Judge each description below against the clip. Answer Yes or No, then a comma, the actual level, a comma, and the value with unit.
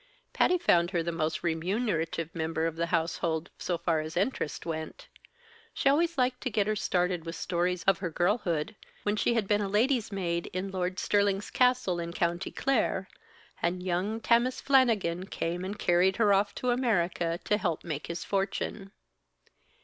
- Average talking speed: Yes, average, 170 wpm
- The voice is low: No, medium, 185 Hz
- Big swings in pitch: No, average, 3.8 semitones